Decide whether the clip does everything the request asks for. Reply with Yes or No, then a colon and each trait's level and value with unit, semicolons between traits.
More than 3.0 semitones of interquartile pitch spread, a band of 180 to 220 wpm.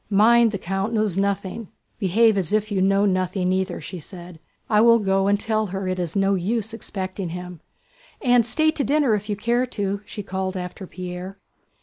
No: average, 2.7 semitones; average, 200 wpm